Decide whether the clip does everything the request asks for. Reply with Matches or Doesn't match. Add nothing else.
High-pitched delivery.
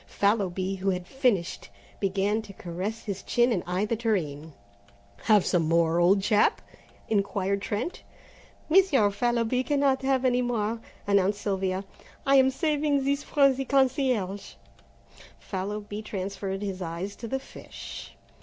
Matches